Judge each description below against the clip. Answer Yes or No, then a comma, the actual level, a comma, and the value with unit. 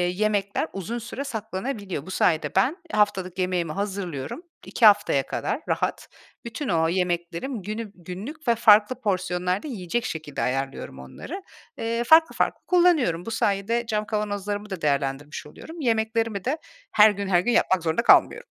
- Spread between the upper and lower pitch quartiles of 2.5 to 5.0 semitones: Yes, average, 4.5 semitones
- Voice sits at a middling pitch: No, high, 205 Hz